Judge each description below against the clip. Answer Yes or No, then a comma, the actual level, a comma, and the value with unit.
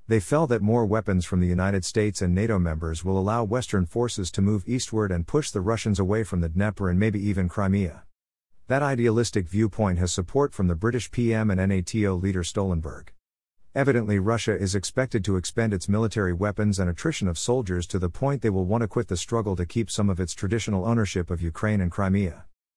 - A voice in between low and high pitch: No, low, 100 Hz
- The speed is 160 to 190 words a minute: No, fast, 205 wpm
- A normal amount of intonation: Yes, average, 3.8 semitones